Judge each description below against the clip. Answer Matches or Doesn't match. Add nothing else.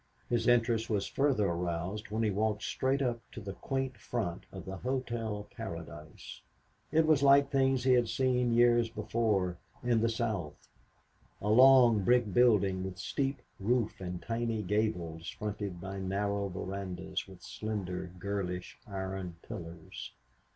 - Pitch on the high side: Doesn't match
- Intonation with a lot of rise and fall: Doesn't match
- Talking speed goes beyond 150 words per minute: Doesn't match